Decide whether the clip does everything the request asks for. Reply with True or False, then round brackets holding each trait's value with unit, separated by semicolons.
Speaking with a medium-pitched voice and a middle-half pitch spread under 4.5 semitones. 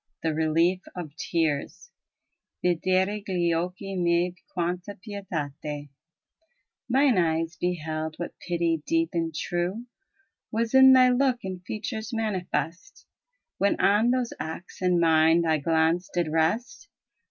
True (175 Hz; 4.1 semitones)